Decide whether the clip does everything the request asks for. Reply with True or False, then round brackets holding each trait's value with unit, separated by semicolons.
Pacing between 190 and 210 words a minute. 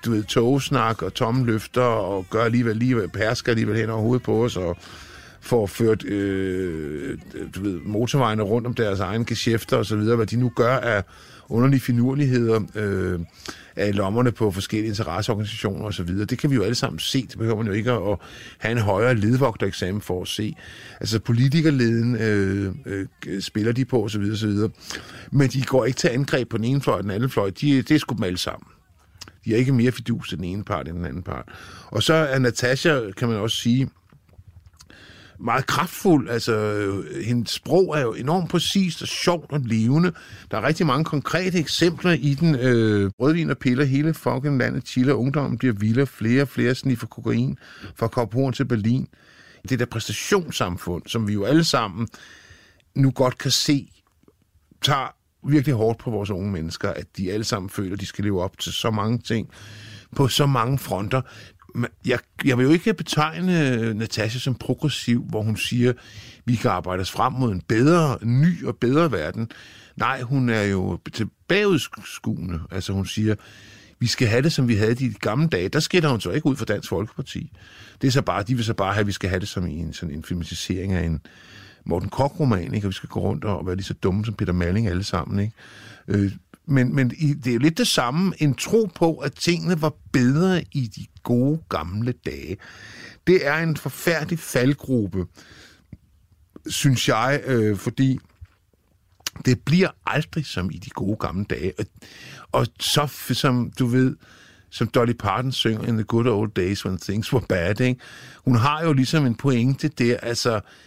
True (195 wpm)